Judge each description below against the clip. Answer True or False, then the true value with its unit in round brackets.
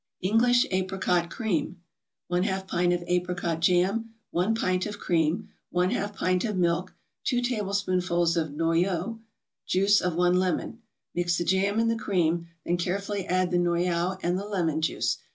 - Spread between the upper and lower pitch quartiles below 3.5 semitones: True (2.4 semitones)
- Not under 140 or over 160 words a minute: True (155 wpm)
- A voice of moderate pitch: True (180 Hz)